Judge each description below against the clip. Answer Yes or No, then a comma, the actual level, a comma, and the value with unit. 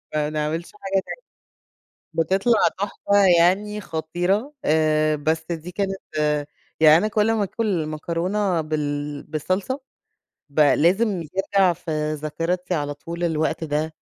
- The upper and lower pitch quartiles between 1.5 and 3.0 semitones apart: No, average, 4.0 semitones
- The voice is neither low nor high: Yes, medium, 165 Hz